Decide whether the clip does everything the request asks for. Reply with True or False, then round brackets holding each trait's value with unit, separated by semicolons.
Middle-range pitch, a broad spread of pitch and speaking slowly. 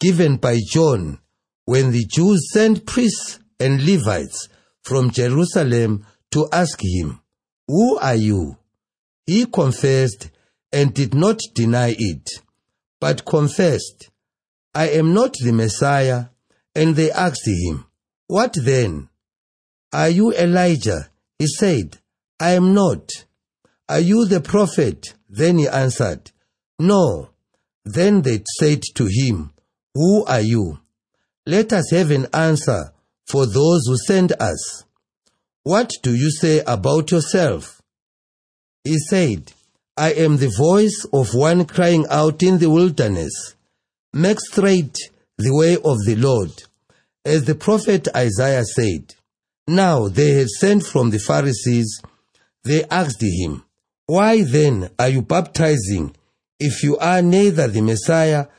True (145 Hz; 7.2 semitones; 125 wpm)